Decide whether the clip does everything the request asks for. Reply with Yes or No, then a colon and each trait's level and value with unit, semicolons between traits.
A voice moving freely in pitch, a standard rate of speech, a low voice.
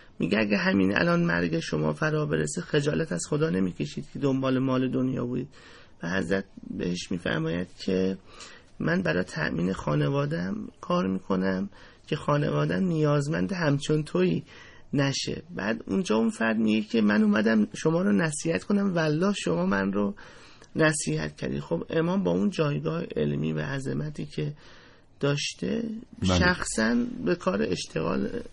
Yes: wide, 9.0 semitones; average, 140 wpm; low, 125 Hz